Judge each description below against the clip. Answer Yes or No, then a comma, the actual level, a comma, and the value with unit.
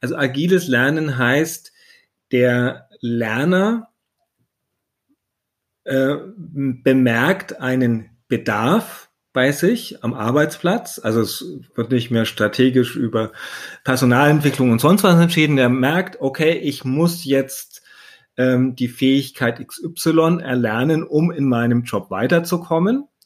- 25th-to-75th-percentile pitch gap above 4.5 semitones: Yes, average, 5.1 semitones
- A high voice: No, low, 135 Hz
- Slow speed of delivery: Yes, slow, 110 wpm